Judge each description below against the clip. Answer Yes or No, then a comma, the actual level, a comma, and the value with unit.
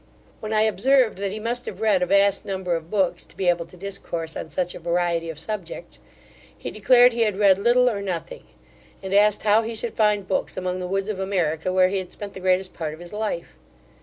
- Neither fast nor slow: No, fast, 230 wpm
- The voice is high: Yes, high, 195 Hz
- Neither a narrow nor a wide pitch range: Yes, average, 3.1 semitones